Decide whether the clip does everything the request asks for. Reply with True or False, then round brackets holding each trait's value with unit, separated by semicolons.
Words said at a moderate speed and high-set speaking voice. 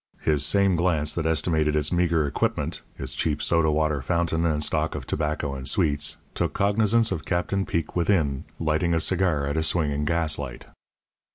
False (170 wpm; 80 Hz)